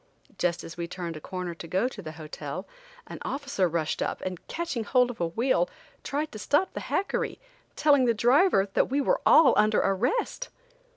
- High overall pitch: Yes, high, 220 Hz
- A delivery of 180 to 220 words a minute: Yes, average, 190 wpm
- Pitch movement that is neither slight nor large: No, wide, 8.4 semitones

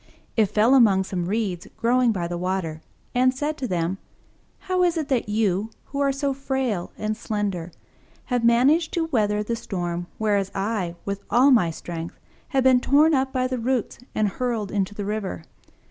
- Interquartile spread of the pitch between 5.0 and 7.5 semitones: Yes, average, 5.3 semitones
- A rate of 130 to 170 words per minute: No, average, 180 wpm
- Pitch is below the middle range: No, high, 220 Hz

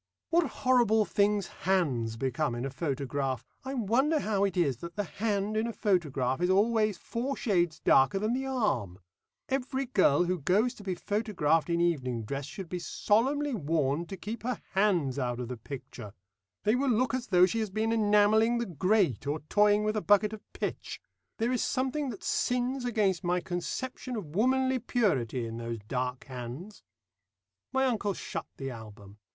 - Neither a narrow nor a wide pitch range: No, wide, 8.2 semitones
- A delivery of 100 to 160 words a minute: No, average, 180 wpm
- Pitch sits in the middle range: No, high, 195 Hz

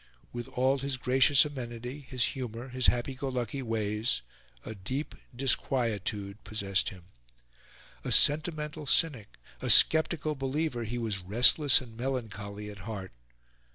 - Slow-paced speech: Yes, slow, 130 wpm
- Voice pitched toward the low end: Yes, low, 125 Hz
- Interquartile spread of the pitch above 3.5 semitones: Yes, average, 4.0 semitones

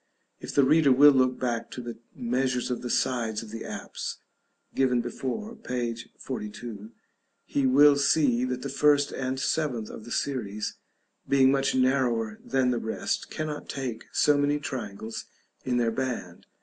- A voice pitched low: Yes, low, 130 Hz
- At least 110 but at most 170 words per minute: Yes, average, 160 wpm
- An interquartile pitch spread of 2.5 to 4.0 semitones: Yes, average, 2.8 semitones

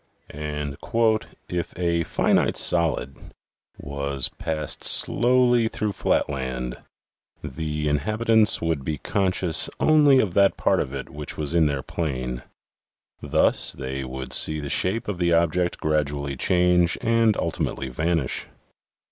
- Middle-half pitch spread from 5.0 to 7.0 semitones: Yes, wide, 5.5 semitones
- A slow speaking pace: Yes, slow, 125 wpm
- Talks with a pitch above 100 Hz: No, very low, 80 Hz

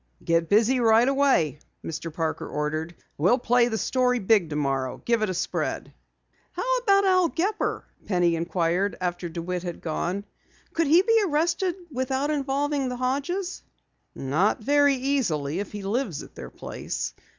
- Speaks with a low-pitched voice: No, high, 225 Hz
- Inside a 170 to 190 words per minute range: No, average, 150 wpm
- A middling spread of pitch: No, wide, 8.8 semitones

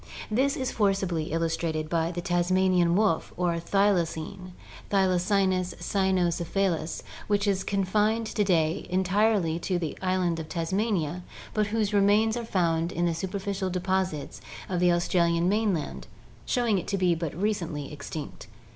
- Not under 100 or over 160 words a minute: Yes, average, 140 wpm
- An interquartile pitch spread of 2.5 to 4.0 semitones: Yes, average, 3.0 semitones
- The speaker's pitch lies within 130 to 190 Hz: Yes, medium, 185 Hz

